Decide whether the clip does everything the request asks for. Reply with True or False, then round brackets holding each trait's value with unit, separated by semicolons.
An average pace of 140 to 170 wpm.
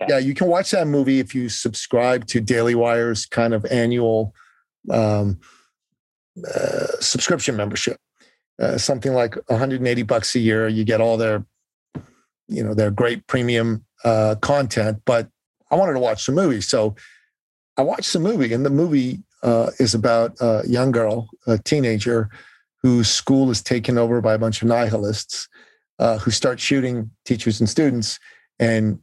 True (160 wpm)